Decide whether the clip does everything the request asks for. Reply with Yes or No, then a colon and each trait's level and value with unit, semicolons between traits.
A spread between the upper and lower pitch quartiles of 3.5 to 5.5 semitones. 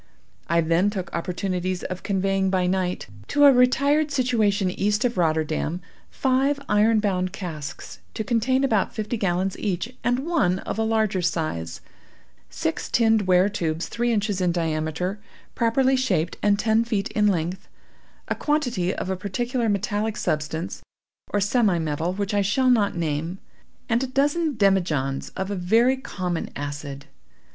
Yes: average, 4.7 semitones